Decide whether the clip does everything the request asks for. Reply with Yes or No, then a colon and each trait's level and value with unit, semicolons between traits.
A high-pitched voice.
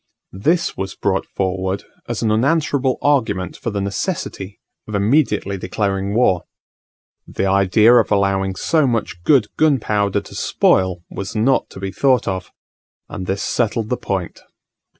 No: low, 100 Hz